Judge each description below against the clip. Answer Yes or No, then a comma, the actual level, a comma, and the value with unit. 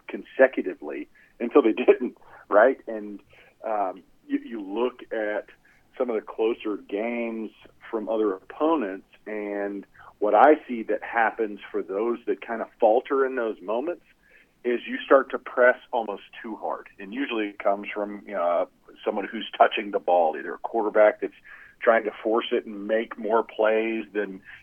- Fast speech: No, average, 160 wpm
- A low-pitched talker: Yes, low, 115 Hz